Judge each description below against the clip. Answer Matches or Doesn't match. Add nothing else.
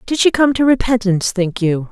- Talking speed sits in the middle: Doesn't match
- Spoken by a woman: Matches